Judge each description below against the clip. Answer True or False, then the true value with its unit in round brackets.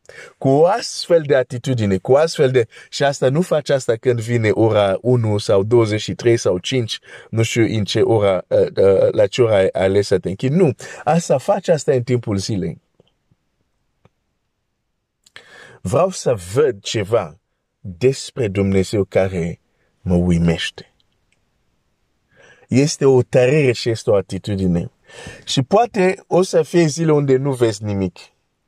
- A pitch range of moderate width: False (5.9 semitones)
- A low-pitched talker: True (120 Hz)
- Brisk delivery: False (140 wpm)